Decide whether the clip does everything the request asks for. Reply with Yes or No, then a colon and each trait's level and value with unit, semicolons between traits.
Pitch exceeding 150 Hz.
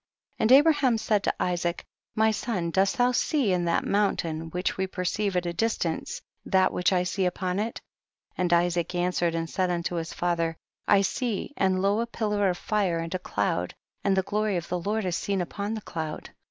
Yes: medium, 185 Hz